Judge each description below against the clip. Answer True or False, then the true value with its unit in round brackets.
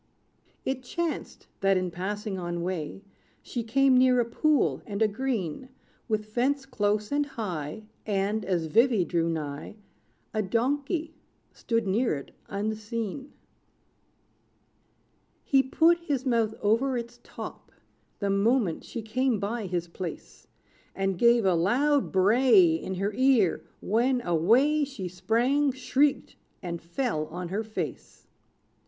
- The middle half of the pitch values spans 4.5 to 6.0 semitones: True (5.5 semitones)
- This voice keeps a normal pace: False (130 wpm)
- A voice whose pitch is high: True (220 Hz)